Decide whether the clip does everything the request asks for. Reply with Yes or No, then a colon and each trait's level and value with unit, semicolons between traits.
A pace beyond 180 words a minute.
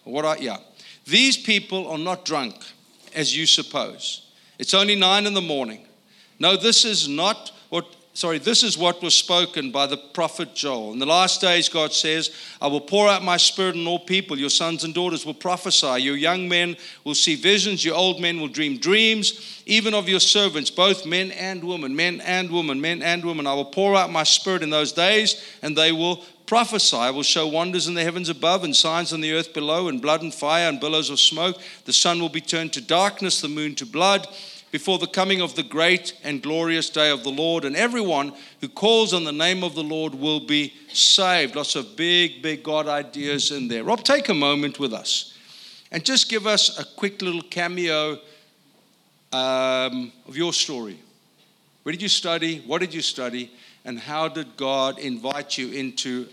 Yes: average, 200 wpm